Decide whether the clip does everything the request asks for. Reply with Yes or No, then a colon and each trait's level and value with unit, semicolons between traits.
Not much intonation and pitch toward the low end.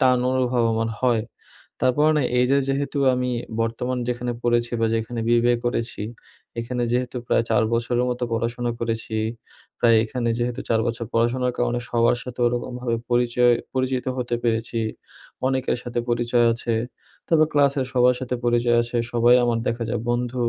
Yes: narrow, 1.2 semitones; low, 120 Hz